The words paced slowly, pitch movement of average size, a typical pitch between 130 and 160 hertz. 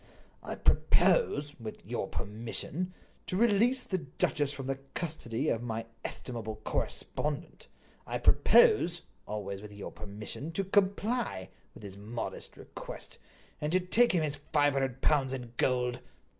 No: slow, 130 wpm; wide, 7.9 semitones; medium, 140 Hz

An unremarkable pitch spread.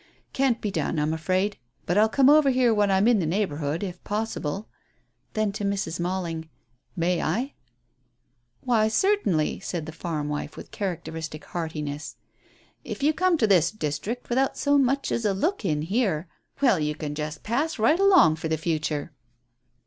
No: wide, 6.9 semitones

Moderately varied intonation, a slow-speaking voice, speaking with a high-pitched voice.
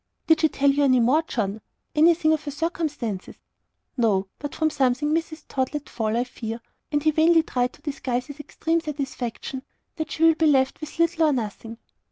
No: average, 4.2 semitones; average, 195 wpm; very high, 290 Hz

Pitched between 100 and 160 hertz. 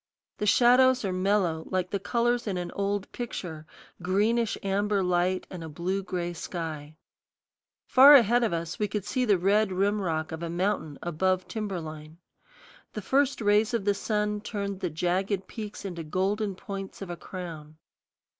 No: high, 195 Hz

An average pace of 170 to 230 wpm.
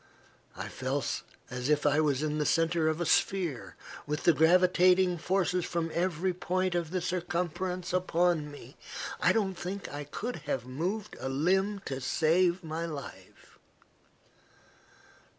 No: average, 145 wpm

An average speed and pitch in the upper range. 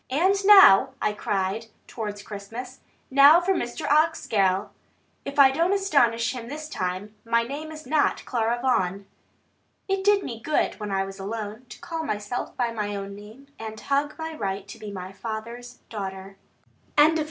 Yes: average, 165 wpm; high, 230 Hz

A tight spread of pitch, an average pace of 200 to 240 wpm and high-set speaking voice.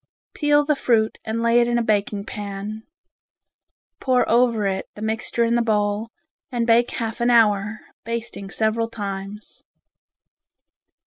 No: narrow, 2.3 semitones; average, 140 wpm; high, 225 Hz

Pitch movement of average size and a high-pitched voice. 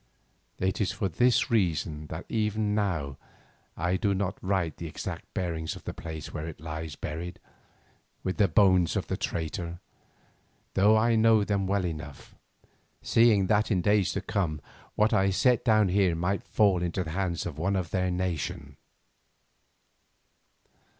No: average, 3.7 semitones; very low, 95 Hz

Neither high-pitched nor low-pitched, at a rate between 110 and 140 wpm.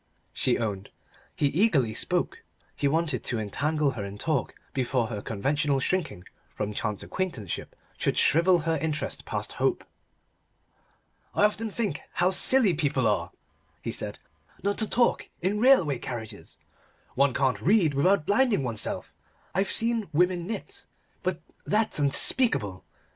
Yes: medium, 150 Hz; slow, 135 wpm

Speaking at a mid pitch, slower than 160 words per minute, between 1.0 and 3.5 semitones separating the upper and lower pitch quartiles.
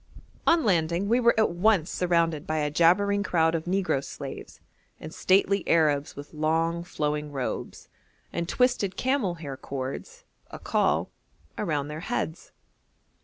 No: medium, 170 Hz; slow, 135 wpm; average, 4.6 semitones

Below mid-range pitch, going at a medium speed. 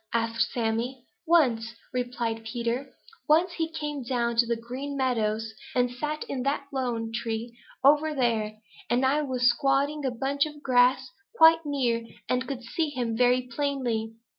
No: very high, 250 Hz; average, 160 wpm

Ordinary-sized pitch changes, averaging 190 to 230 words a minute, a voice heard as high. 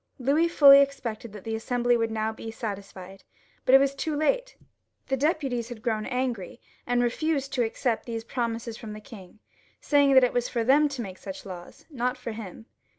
Yes: average, 3.6 semitones; average, 195 wpm; high, 240 Hz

